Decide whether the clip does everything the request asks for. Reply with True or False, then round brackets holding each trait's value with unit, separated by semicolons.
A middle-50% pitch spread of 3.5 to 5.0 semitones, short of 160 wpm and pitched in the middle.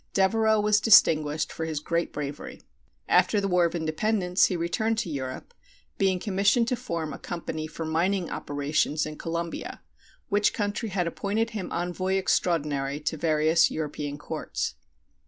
True (4.6 semitones; 150 wpm; 170 Hz)